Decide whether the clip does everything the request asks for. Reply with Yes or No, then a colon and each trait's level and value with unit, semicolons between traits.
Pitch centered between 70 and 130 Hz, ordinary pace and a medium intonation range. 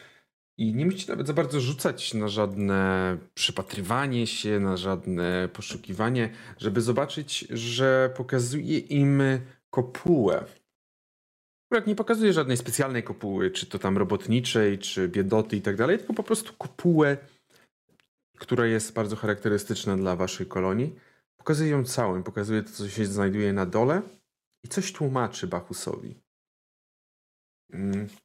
No: low, 115 Hz; average, 130 wpm; wide, 5.7 semitones